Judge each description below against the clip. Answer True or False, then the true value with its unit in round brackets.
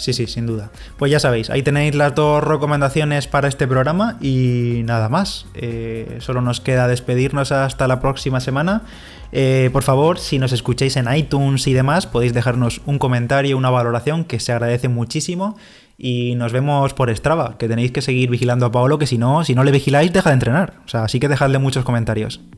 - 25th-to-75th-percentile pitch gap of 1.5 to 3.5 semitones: True (2.9 semitones)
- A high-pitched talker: False (130 Hz)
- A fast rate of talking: True (200 wpm)